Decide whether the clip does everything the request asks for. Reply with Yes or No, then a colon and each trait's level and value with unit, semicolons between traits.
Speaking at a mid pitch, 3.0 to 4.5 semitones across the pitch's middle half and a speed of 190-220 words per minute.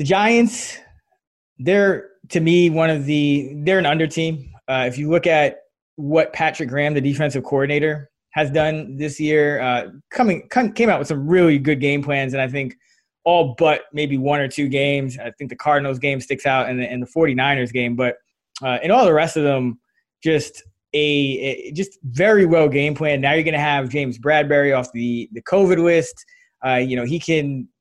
Yes: medium, 145 Hz; average, 3.3 semitones; average, 195 wpm